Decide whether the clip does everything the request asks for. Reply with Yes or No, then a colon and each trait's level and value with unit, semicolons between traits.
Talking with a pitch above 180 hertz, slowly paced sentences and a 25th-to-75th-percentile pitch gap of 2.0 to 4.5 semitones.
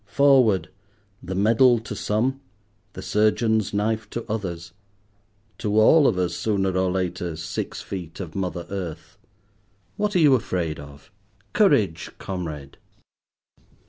No: low, 100 Hz; slow, 125 wpm; average, 4.2 semitones